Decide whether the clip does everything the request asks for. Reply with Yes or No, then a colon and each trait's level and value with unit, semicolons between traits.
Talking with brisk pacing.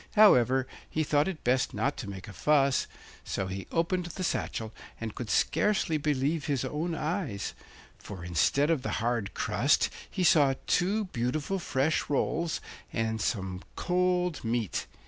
No: average, 150 wpm